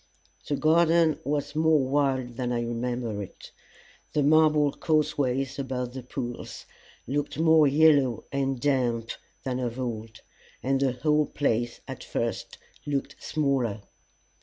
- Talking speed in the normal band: No, slow, 130 wpm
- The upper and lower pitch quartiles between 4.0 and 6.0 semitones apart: No, average, 3.3 semitones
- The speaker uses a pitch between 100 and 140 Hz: Yes, low, 135 Hz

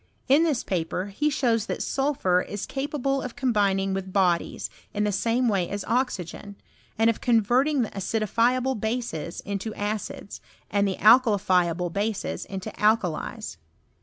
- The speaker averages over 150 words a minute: No, average, 145 wpm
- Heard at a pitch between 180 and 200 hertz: No, high, 215 Hz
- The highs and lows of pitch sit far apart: No, average, 4.3 semitones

